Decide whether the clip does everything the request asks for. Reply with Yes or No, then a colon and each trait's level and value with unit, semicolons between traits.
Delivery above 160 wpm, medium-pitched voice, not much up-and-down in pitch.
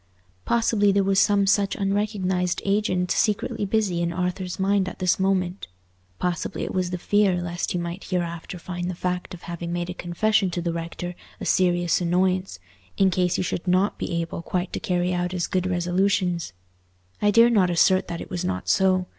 Yes: average, 190 wpm; medium, 180 Hz; narrow, 1.8 semitones